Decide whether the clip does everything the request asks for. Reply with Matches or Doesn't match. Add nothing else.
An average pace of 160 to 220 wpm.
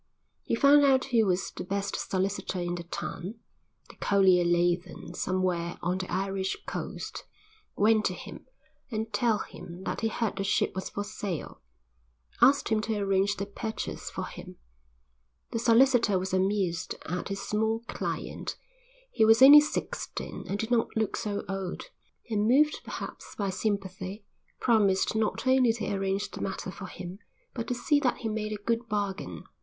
Matches